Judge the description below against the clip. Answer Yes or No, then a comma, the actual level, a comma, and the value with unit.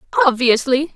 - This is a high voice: Yes, very high, 270 Hz